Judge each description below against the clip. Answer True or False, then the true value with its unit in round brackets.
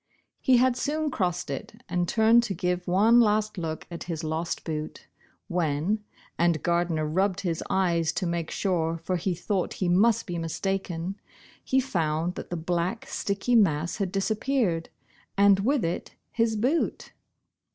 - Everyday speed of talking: True (160 wpm)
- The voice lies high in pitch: False (180 Hz)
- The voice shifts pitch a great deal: False (4.2 semitones)